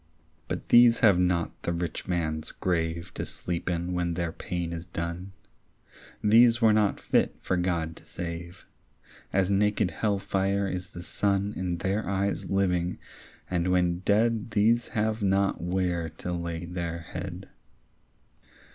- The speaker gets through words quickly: No, average, 145 wpm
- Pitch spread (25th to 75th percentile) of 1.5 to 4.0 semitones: Yes, average, 2.7 semitones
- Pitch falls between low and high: No, very low, 90 Hz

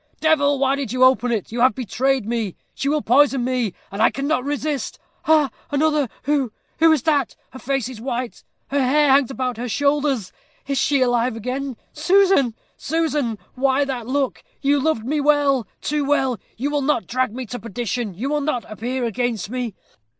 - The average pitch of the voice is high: Yes, very high, 265 Hz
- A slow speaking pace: No, average, 185 wpm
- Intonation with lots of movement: No, average, 3.0 semitones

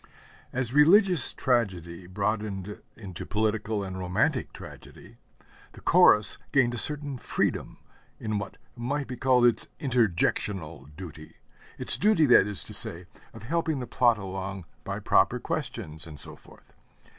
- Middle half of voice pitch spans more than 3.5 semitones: Yes, wide, 5.4 semitones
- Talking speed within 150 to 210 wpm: No, average, 140 wpm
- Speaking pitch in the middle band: No, low, 110 Hz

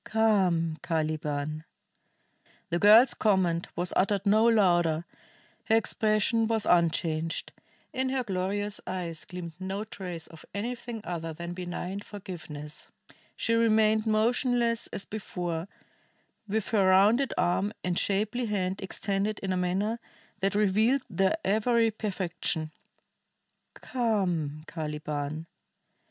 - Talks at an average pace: No, slow, 115 wpm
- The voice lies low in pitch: No, high, 195 Hz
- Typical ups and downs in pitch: Yes, average, 4.2 semitones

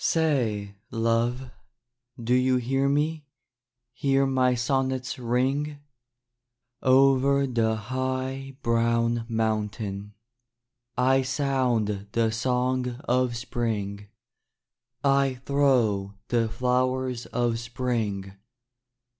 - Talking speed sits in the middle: No, slow, 85 wpm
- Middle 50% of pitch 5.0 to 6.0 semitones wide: No, narrow, 2.5 semitones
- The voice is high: No, low, 125 Hz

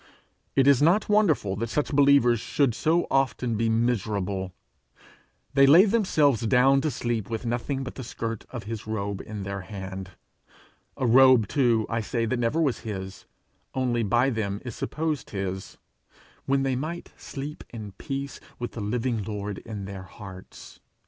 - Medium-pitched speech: No, low, 120 Hz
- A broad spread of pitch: No, average, 4.7 semitones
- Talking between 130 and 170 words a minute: Yes, average, 160 wpm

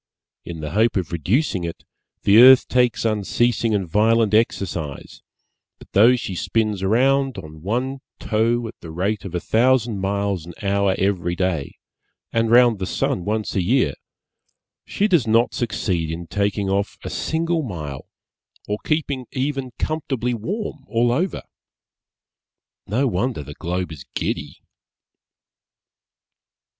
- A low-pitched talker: Yes, low, 110 Hz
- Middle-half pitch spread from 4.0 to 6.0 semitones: Yes, average, 5.0 semitones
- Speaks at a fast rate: No, average, 140 wpm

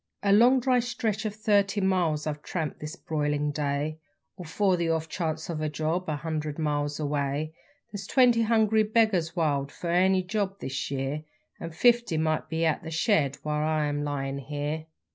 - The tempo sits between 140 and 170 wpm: No, average, 180 wpm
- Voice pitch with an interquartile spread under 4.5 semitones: No, average, 4.9 semitones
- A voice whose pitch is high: No, medium, 160 Hz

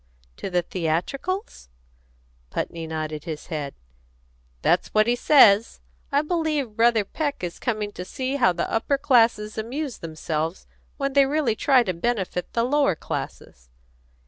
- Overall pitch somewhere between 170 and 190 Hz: No, high, 220 Hz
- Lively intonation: Yes, wide, 7.9 semitones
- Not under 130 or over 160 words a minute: Yes, average, 145 wpm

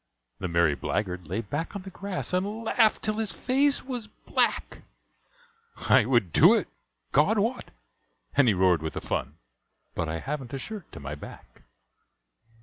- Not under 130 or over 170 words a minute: Yes, average, 165 wpm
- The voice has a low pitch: No, medium, 145 Hz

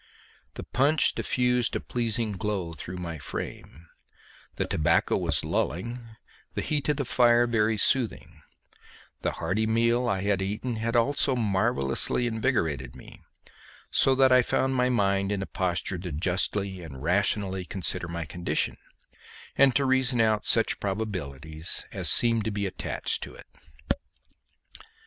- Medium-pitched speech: No, low, 105 Hz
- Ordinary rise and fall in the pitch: Yes, average, 5.0 semitones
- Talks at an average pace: Yes, average, 145 wpm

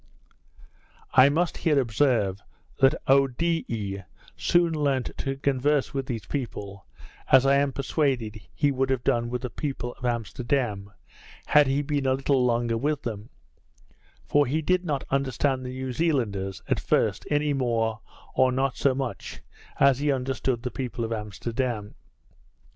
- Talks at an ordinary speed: Yes, average, 150 wpm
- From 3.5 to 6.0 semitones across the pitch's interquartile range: No, average, 3.1 semitones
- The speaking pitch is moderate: No, low, 130 Hz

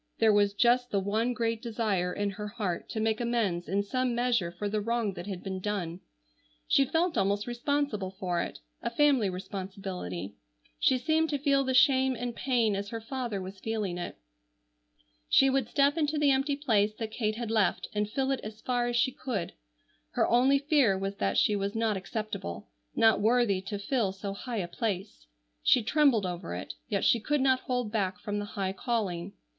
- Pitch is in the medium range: No, high, 215 Hz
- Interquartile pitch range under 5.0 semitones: Yes, average, 4.2 semitones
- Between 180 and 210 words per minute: Yes, average, 195 wpm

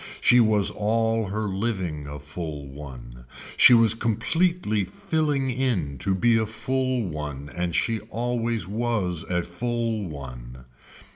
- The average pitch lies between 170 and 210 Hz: No, low, 105 Hz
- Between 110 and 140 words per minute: Yes, slow, 135 wpm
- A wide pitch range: Yes, wide, 7.5 semitones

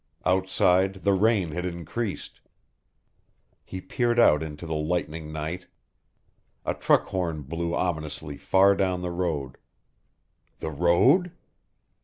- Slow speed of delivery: Yes, slow, 115 wpm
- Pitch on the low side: Yes, very low, 90 Hz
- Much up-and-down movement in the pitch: No, average, 3.4 semitones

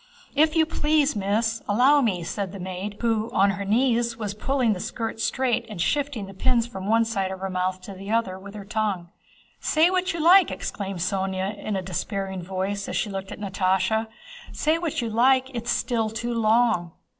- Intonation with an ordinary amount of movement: Yes, average, 3.9 semitones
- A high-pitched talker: Yes, high, 215 Hz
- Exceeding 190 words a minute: Yes, average, 200 wpm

